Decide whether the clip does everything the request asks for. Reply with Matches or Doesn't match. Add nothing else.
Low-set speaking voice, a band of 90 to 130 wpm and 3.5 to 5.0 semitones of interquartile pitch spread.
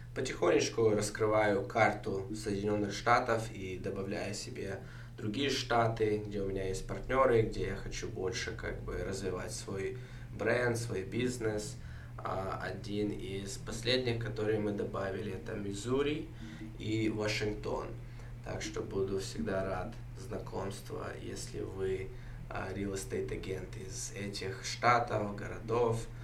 Doesn't match